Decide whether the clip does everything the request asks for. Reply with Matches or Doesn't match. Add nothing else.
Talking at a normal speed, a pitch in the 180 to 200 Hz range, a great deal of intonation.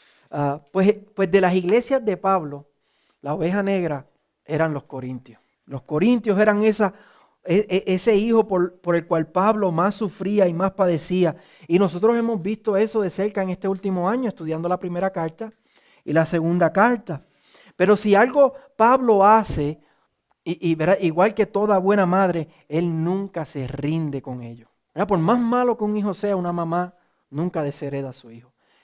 Doesn't match